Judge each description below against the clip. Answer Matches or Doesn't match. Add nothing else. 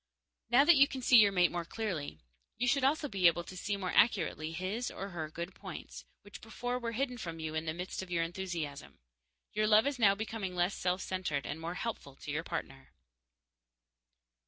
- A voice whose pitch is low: Doesn't match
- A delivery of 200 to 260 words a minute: Matches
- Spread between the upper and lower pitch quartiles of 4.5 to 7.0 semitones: Matches